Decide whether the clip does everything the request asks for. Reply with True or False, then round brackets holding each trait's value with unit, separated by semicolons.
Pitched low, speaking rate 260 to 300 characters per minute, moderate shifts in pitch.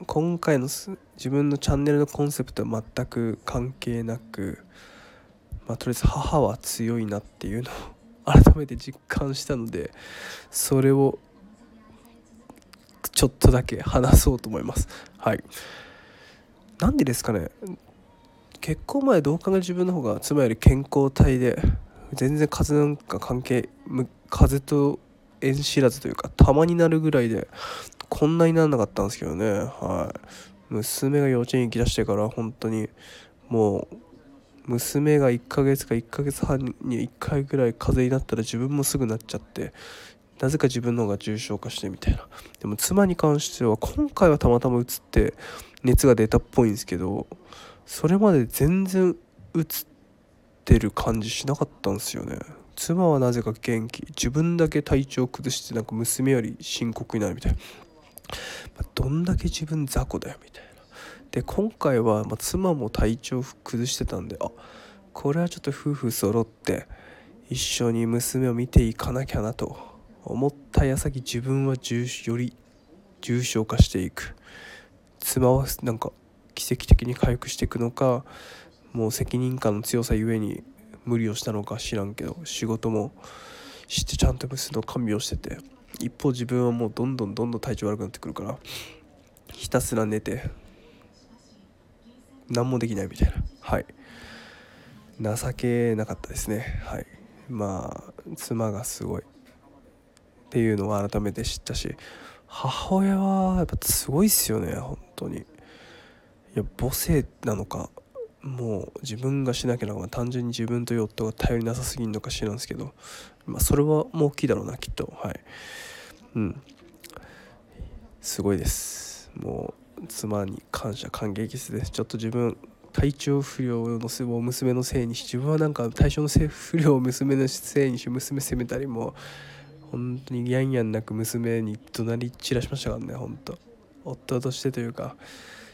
True (125 Hz; 295 characters per minute; 3.9 semitones)